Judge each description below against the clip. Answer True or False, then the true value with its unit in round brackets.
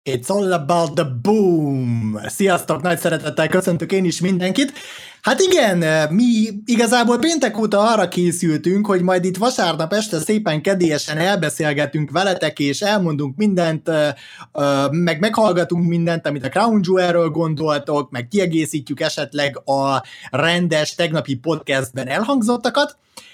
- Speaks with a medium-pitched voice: True (170 Hz)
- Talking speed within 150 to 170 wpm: False (125 wpm)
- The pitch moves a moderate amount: True (4.9 semitones)